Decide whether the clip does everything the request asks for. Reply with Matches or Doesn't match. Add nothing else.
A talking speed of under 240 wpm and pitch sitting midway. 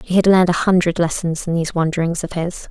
Doesn't match